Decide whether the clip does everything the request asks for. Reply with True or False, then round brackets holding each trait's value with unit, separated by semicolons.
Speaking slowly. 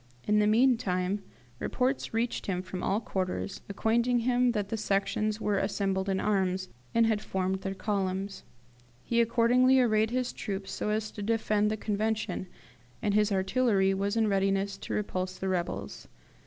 False (160 wpm)